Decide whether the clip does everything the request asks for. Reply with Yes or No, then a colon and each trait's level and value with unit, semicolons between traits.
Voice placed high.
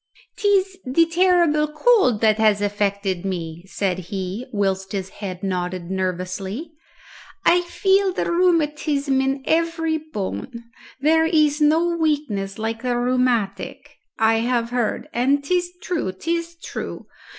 Yes: very high, 250 Hz